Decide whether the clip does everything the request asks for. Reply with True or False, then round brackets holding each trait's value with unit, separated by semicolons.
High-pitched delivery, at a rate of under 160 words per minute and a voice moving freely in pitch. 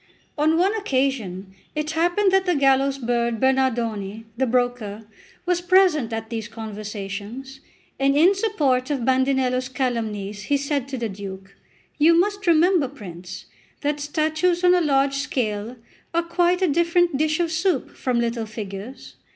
True (270 Hz; 150 wpm; 6.4 semitones)